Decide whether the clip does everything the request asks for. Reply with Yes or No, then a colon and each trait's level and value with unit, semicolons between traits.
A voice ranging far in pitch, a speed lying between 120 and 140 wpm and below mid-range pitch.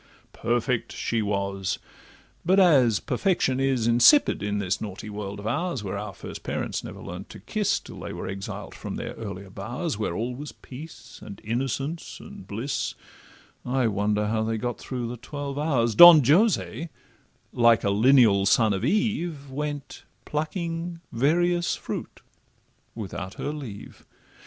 No: wide, 6.3 semitones; average, 150 wpm; low, 120 Hz